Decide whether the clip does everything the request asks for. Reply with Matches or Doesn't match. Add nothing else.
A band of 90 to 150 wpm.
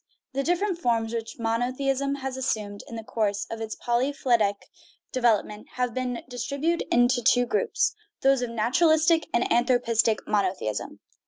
Matches